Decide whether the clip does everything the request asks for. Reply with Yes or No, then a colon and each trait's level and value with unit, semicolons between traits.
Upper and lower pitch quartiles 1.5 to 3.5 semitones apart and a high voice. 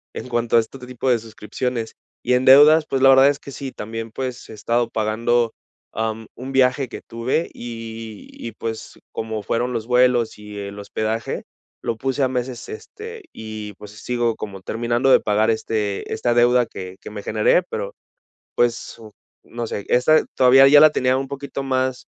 No: average, 2.9 semitones; low, 120 Hz